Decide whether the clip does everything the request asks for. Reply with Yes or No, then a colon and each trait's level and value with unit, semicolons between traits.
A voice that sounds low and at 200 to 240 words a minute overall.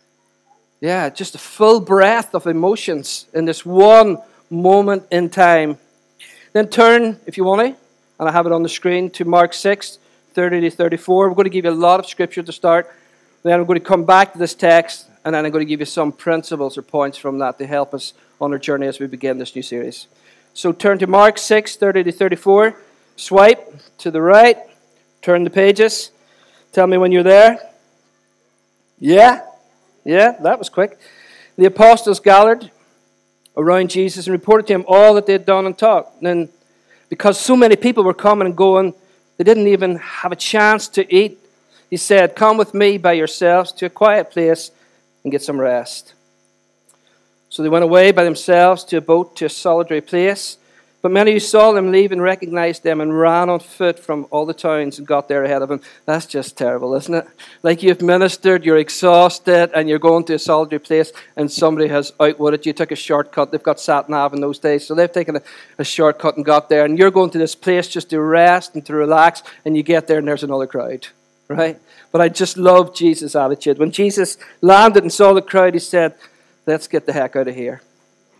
No: medium, 175 Hz; fast, 205 wpm